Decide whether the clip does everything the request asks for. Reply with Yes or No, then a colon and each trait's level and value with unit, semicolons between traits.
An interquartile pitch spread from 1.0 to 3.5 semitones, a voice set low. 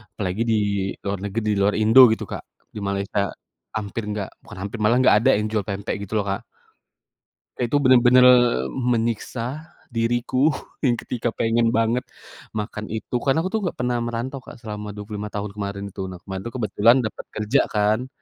Yes: average, 2.7 semitones; low, 110 Hz